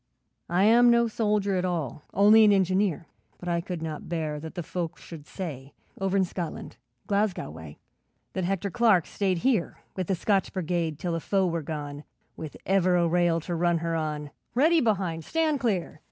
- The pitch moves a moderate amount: Yes, average, 3.5 semitones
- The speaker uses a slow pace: No, average, 185 wpm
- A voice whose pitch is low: No, medium, 180 Hz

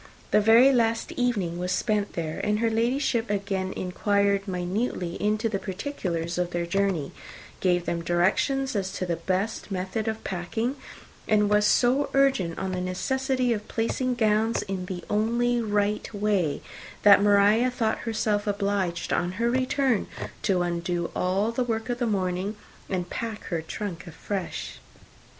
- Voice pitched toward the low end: No, high, 205 Hz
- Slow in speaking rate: No, average, 155 wpm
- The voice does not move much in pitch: No, average, 3.8 semitones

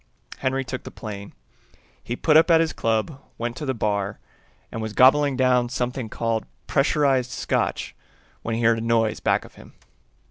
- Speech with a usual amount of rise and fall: Yes, average, 3.1 semitones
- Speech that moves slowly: No, average, 175 wpm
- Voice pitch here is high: No, low, 125 Hz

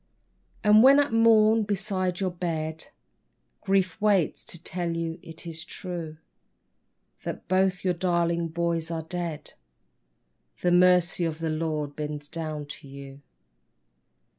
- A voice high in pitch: No, medium, 170 Hz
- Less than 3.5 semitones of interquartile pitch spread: Yes, narrow, 2.6 semitones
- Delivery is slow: Yes, slow, 130 wpm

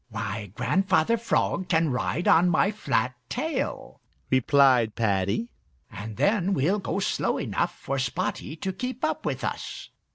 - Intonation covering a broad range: Yes, wide, 8.9 semitones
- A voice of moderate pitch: Yes, medium, 155 Hz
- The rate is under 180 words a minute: Yes, average, 140 wpm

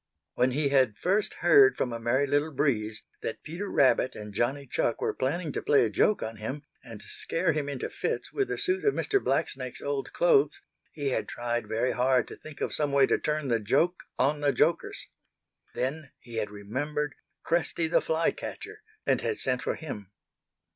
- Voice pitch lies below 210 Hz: Yes, medium, 140 Hz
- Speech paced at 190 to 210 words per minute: Yes, average, 195 wpm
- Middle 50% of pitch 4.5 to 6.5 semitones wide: Yes, average, 5.1 semitones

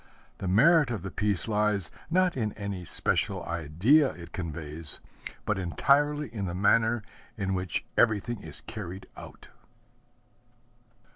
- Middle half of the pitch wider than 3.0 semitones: Yes, average, 5.0 semitones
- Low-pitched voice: Yes, low, 100 Hz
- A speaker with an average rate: No, slow, 130 wpm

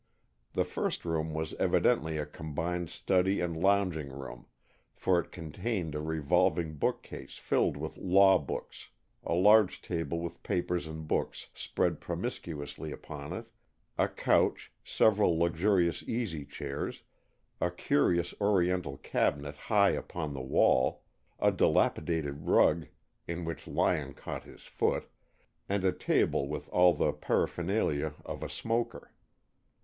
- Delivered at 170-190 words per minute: No, slow, 135 wpm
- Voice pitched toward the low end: Yes, very low, 85 Hz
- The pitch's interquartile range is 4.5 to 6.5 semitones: No, average, 3.4 semitones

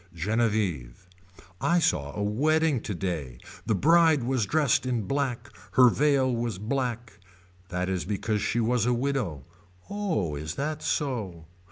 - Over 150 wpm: No, average, 140 wpm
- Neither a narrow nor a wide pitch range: No, wide, 6.5 semitones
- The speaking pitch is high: No, low, 115 Hz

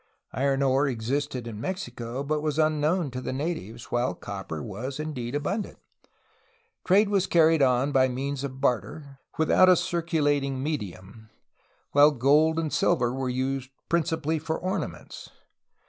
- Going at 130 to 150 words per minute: Yes, average, 145 wpm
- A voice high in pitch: No, medium, 140 Hz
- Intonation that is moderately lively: Yes, average, 3.8 semitones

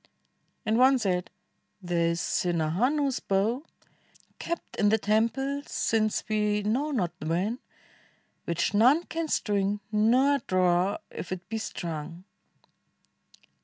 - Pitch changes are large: Yes, wide, 5.8 semitones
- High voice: Yes, high, 210 Hz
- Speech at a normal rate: No, slow, 115 wpm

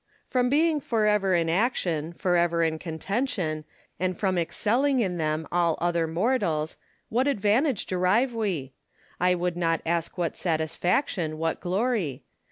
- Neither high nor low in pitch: Yes, medium, 180 Hz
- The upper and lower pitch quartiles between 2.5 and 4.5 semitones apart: No, average, 5.2 semitones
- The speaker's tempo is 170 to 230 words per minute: No, average, 155 wpm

